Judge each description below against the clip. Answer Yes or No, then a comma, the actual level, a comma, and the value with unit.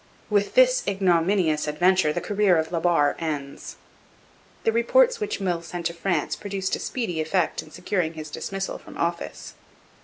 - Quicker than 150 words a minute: Yes, average, 160 wpm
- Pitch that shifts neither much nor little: Yes, average, 3.9 semitones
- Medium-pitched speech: Yes, medium, 180 Hz